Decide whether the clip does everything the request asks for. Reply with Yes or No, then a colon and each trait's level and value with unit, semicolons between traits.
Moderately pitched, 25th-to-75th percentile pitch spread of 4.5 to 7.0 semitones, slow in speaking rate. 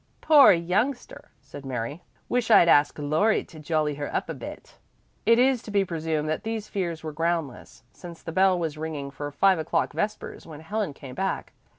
No: medium, 165 Hz; average, 5.1 semitones; average, 190 wpm